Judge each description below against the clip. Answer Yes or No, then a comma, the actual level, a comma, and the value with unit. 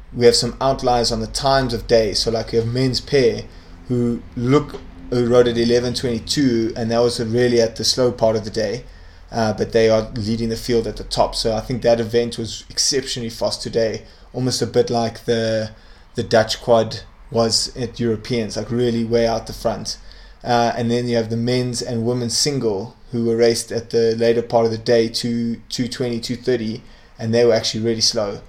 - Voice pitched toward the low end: Yes, low, 115 Hz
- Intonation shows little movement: Yes, narrow, 1.3 semitones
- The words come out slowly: No, fast, 205 wpm